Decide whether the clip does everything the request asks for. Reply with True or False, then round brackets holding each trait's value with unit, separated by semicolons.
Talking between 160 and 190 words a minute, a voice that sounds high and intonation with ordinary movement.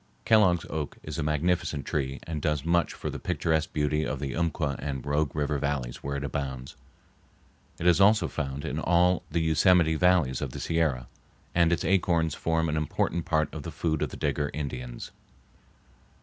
False (180 wpm; 75 Hz; 3.0 semitones)